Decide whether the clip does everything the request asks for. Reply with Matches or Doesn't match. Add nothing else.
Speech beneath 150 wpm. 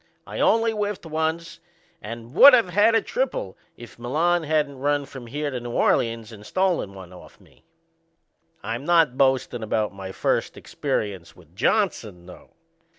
Doesn't match